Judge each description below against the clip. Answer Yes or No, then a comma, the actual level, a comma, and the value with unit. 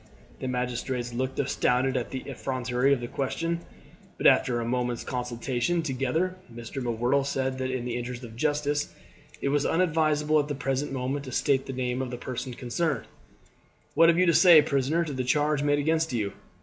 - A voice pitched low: Yes, low, 130 Hz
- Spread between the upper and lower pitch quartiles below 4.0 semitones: Yes, average, 2.9 semitones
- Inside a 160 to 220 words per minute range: Yes, average, 190 wpm